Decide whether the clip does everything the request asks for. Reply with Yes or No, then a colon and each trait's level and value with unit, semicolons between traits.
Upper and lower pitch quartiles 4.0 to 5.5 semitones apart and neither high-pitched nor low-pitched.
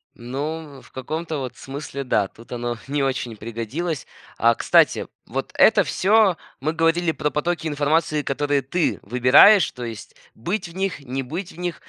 Yes: average, 4.7 semitones; medium, 145 Hz